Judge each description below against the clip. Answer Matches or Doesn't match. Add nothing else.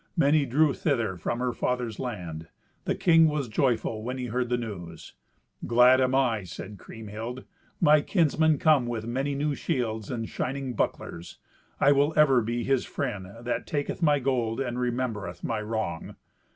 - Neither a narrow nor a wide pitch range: Matches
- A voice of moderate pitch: Doesn't match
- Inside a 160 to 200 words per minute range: Matches